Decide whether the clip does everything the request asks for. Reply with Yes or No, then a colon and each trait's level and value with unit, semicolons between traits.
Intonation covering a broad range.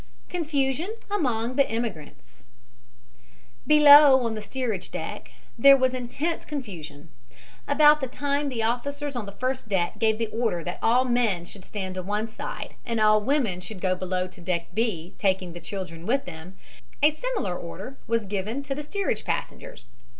Yes: wide, 6.6 semitones